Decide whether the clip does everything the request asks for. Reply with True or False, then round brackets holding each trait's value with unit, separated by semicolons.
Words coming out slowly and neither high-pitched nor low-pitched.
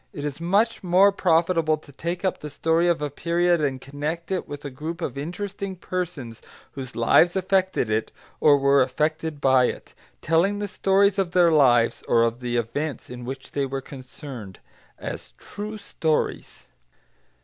False (170 wpm; 155 Hz)